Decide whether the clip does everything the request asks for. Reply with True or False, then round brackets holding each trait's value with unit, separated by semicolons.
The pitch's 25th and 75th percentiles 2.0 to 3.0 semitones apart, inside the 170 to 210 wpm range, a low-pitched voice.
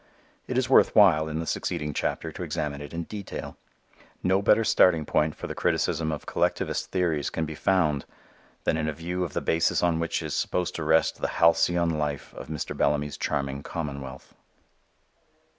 True (2.4 semitones; 180 wpm; 80 Hz)